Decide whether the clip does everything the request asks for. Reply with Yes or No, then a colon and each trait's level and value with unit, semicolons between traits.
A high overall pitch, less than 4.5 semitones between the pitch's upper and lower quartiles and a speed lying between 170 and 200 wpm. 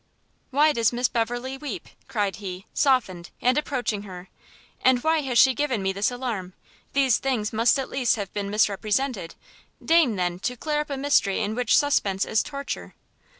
No: high, 240 Hz; average, 5.0 semitones; average, 175 wpm